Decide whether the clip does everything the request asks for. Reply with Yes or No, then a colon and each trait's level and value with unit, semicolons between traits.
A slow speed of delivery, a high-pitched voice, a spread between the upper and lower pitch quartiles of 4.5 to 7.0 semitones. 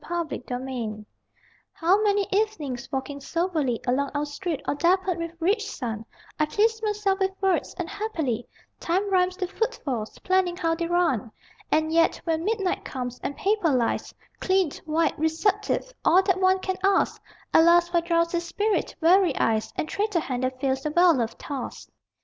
No: average, 165 wpm; very high, 340 Hz; average, 5.3 semitones